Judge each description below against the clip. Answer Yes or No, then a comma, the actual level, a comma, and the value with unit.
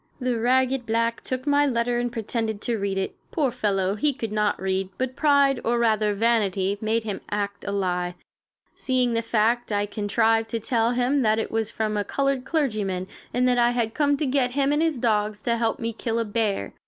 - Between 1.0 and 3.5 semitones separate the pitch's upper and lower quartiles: Yes, average, 3.2 semitones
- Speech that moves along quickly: Yes, fast, 210 wpm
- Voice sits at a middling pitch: No, high, 230 Hz